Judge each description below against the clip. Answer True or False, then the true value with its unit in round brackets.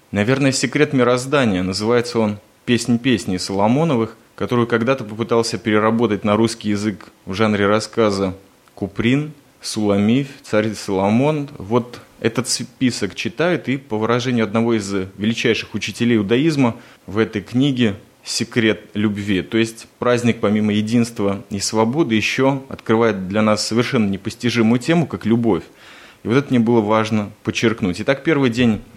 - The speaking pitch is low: True (115 Hz)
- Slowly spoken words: False (135 wpm)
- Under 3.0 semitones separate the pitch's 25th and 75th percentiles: True (2.6 semitones)